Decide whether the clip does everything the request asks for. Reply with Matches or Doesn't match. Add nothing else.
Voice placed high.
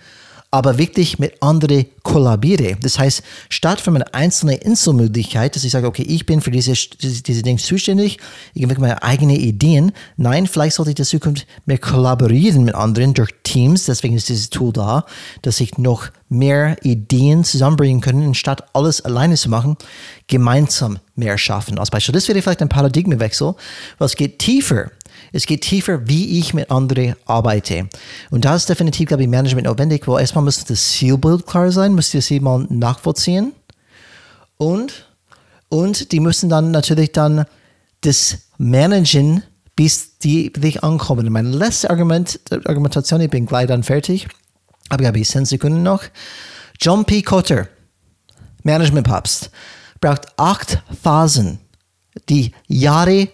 Doesn't match